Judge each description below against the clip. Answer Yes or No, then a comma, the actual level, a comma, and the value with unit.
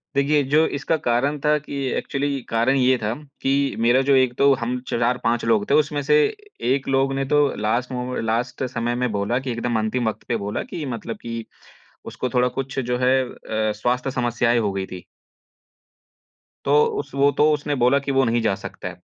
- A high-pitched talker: No, low, 125 Hz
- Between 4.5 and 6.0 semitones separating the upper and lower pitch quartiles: No, average, 2.8 semitones